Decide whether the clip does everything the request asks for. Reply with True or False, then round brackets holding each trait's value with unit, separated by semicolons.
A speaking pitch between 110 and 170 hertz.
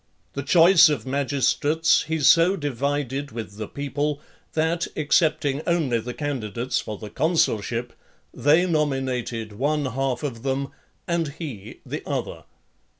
True (140 Hz)